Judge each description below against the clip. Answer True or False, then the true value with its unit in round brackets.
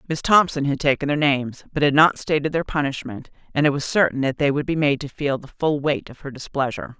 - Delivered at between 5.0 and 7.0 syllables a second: True (6.0 syllables/s)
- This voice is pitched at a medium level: True (145 Hz)